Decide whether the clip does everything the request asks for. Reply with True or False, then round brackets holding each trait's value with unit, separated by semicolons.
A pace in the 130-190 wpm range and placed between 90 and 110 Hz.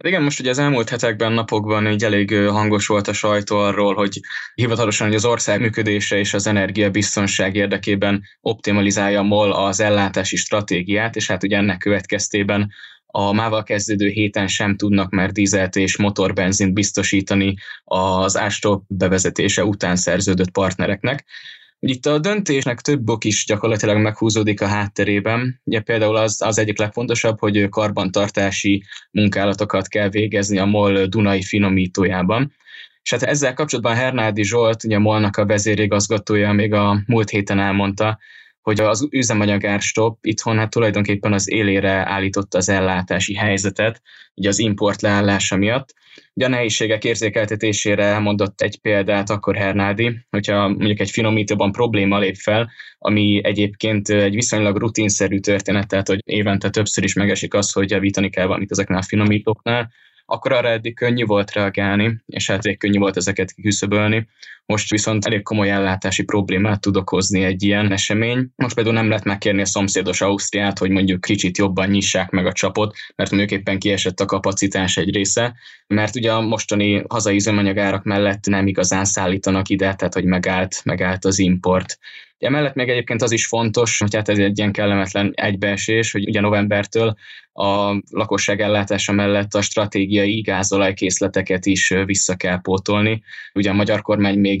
True (155 wpm; 105 Hz)